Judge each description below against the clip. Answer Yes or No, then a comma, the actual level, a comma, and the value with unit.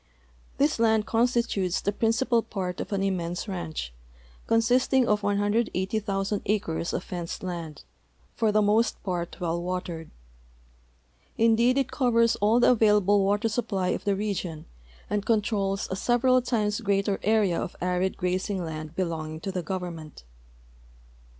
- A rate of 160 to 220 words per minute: No, average, 140 wpm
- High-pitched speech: Yes, high, 200 Hz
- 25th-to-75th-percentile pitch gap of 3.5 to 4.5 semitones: Yes, average, 3.9 semitones